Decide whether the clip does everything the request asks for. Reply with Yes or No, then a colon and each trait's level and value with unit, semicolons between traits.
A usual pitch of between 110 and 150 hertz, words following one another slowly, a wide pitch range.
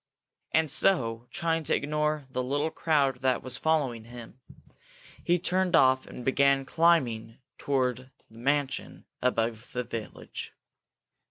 No: low, 135 Hz; slow, 125 wpm; average, 3.9 semitones